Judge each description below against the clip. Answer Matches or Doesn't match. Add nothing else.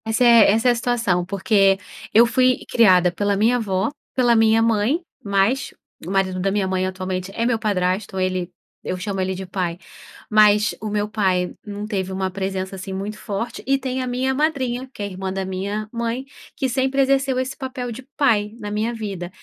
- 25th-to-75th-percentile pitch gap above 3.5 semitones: Matches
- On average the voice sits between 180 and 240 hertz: Matches